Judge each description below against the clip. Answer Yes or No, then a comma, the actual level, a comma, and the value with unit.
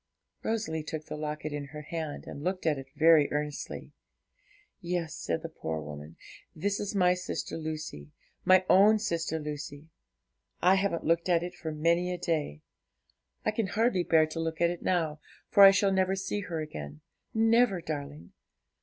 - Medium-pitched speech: Yes, medium, 165 Hz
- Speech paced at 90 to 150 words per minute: No, average, 170 wpm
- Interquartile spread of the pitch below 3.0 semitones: No, average, 3.7 semitones